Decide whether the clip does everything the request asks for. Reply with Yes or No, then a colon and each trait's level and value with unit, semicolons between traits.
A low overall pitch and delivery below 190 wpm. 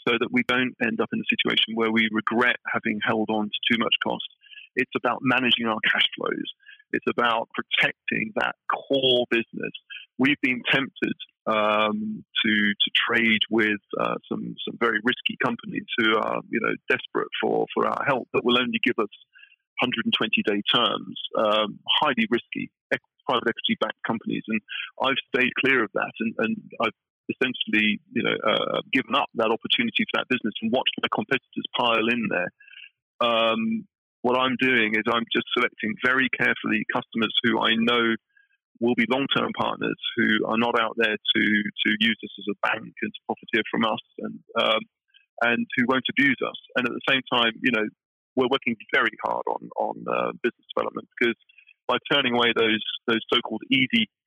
Yes: low, 120 Hz; average, 180 wpm